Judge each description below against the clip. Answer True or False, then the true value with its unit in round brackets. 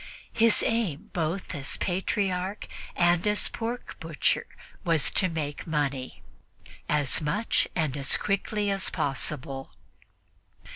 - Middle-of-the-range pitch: True (170 Hz)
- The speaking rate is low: True (110 wpm)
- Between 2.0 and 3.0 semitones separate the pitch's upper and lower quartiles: False (5.3 semitones)